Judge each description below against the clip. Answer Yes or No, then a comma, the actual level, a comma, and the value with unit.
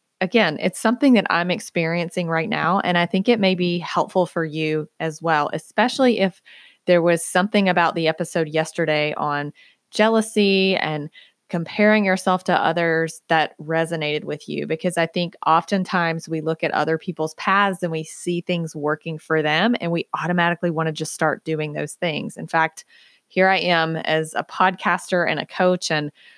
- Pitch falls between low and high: Yes, medium, 170 Hz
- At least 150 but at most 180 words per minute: Yes, average, 175 wpm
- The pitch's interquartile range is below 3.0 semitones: Yes, narrow, 2.6 semitones